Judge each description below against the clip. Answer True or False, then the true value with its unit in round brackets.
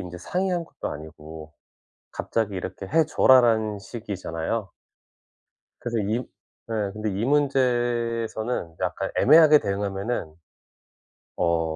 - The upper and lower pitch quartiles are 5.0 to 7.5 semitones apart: False (4.6 semitones)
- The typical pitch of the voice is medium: False (110 Hz)